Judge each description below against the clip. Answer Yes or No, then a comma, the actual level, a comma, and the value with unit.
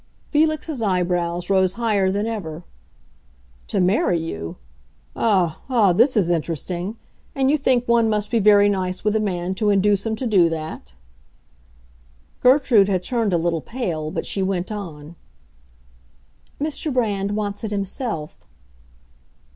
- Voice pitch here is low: No, high, 200 Hz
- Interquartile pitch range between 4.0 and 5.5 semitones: Yes, average, 4.4 semitones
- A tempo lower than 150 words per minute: Yes, average, 140 wpm